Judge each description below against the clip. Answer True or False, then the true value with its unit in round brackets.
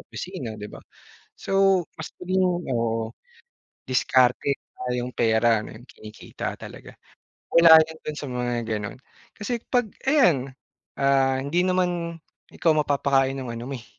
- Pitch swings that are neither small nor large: False (5.8 semitones)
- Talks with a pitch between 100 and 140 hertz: True (135 Hz)